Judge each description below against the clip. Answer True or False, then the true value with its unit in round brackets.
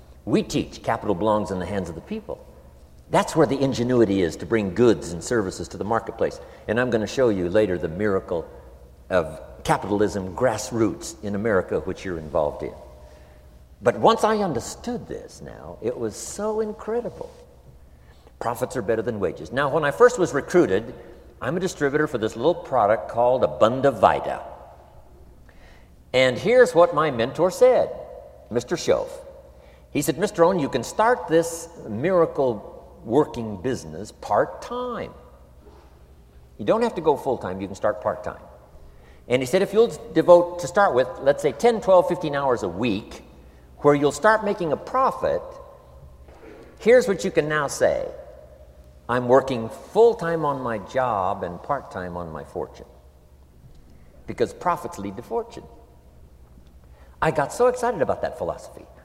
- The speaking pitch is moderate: False (115 Hz)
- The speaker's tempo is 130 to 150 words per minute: False (160 wpm)